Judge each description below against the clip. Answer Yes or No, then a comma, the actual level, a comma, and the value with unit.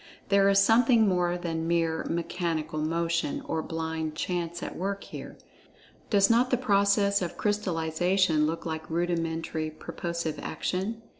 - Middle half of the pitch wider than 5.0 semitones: No, average, 3.5 semitones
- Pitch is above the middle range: No, medium, 170 Hz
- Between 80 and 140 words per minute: Yes, slow, 135 wpm